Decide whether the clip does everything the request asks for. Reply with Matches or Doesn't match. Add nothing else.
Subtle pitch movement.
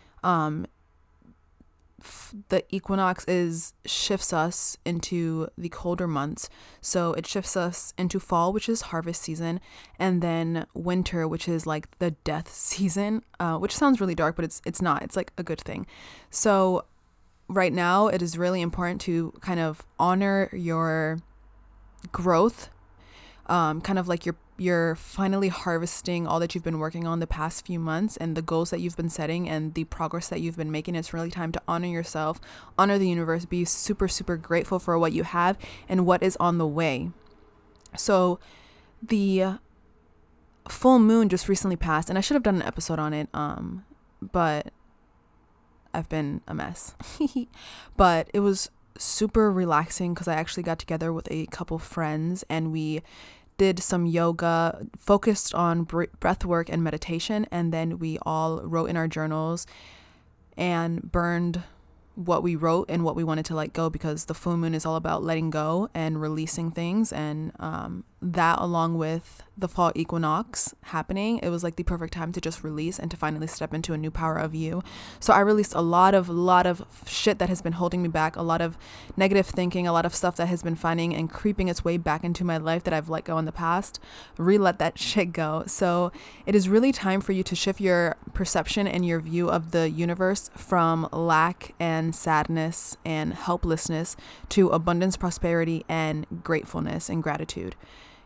Matches